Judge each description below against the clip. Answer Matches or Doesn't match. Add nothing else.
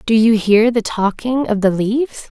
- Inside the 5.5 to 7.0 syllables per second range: Doesn't match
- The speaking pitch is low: Doesn't match